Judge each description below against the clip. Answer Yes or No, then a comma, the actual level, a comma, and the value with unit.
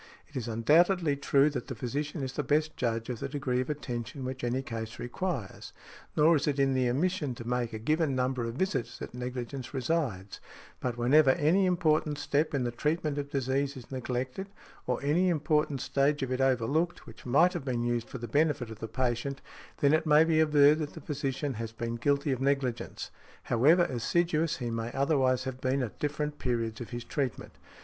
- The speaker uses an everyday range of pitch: Yes, average, 3.6 semitones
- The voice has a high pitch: No, low, 135 Hz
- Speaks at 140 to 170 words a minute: No, average, 200 wpm